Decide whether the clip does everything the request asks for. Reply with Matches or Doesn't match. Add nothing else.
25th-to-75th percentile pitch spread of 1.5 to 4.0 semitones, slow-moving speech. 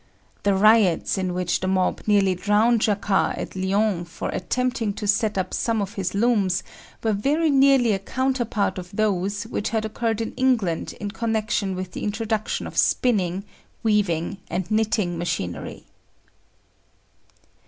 Doesn't match